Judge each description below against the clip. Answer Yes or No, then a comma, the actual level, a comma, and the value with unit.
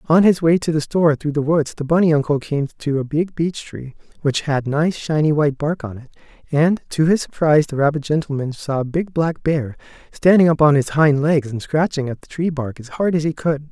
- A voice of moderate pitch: Yes, medium, 150 Hz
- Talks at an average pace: No, fast, 240 wpm